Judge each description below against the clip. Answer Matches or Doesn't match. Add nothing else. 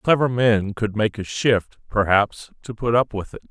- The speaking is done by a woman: Doesn't match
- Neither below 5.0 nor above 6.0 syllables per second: Doesn't match